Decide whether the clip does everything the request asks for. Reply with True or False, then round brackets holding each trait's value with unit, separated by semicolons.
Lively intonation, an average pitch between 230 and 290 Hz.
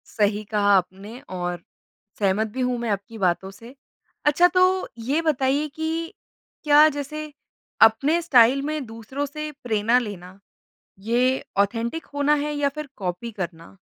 True (6.4 semitones; 235 Hz)